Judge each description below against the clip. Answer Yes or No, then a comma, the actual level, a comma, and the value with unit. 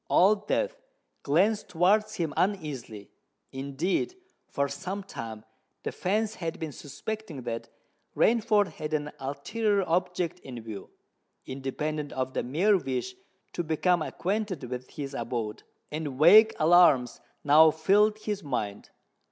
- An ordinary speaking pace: No, slow, 125 wpm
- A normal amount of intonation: No, wide, 6.7 semitones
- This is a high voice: No, medium, 160 Hz